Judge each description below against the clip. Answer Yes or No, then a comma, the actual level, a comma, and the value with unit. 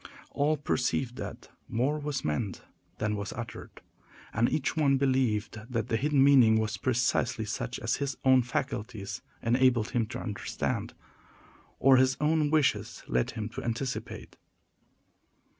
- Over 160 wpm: No, average, 140 wpm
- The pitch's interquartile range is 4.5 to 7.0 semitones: No, average, 3.7 semitones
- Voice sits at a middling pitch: No, low, 125 Hz